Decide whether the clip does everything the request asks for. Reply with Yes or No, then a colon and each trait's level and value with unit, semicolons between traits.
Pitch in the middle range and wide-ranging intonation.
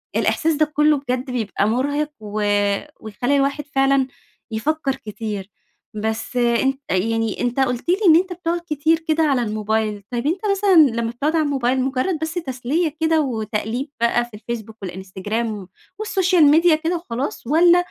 No: very high, 265 Hz; wide, 5.7 semitones